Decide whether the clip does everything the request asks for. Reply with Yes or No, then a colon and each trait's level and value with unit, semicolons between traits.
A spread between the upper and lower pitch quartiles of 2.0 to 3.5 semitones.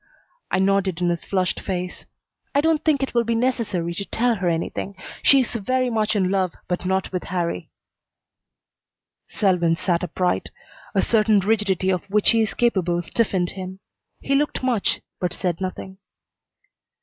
No: average, 4.0 semitones